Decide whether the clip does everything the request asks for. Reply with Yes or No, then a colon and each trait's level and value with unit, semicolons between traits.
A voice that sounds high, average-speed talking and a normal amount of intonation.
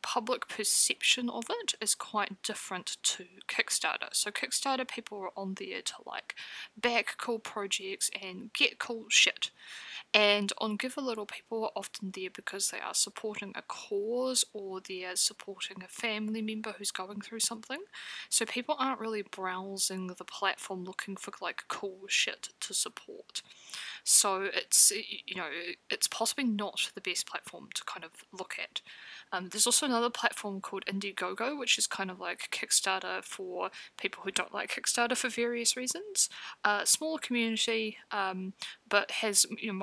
Yes: high, 220 Hz; average, 165 wpm; average, 3.8 semitones